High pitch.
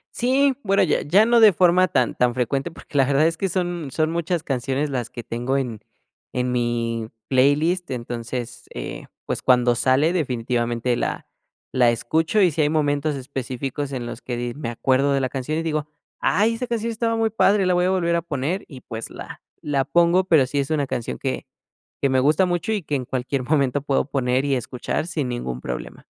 No: medium, 140 Hz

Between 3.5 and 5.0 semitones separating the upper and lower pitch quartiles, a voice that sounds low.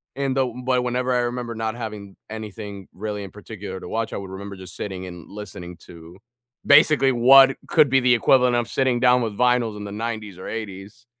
Yes: average, 3.8 semitones; low, 110 Hz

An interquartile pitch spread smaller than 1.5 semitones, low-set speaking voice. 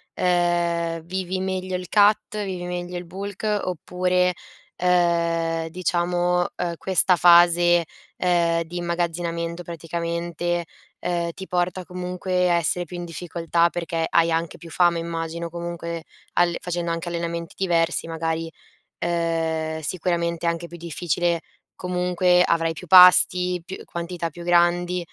No: narrow, 1.1 semitones; medium, 175 Hz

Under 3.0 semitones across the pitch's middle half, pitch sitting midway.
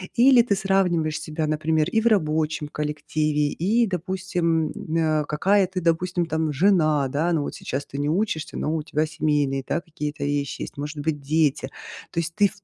No: average, 3.3 semitones; medium, 160 Hz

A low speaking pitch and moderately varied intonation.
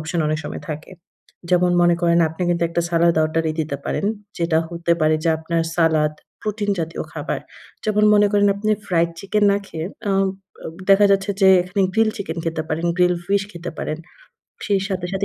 No: medium, 175 Hz; average, 3.3 semitones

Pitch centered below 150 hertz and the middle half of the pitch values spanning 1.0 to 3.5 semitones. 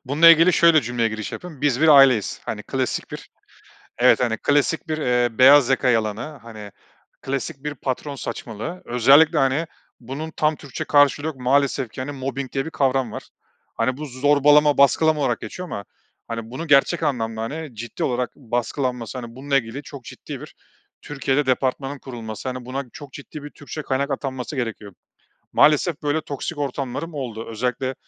Yes: low, 135 Hz; average, 3.1 semitones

